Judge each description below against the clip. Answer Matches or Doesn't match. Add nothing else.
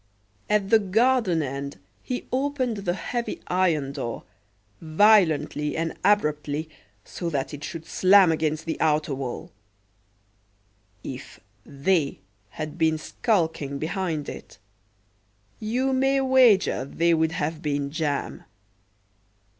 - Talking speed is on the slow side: Matches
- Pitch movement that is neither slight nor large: Doesn't match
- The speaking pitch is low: Doesn't match